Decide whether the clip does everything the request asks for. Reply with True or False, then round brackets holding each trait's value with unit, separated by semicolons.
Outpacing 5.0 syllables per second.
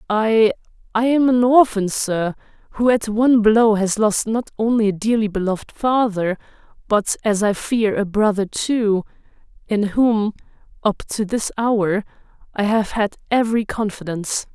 False (4.5 syllables/s)